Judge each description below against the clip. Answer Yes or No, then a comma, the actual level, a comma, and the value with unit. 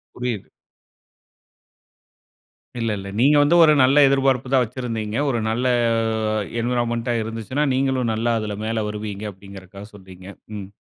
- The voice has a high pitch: No, low, 115 Hz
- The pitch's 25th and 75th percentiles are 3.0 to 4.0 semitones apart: Yes, average, 3.5 semitones